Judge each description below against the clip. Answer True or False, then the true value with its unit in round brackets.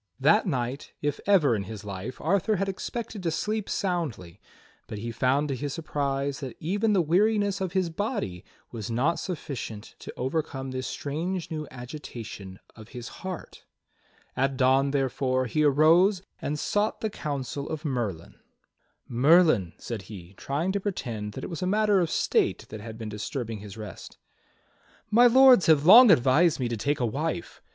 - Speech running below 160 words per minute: False (170 wpm)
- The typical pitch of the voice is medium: True (145 Hz)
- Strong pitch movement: True (7.3 semitones)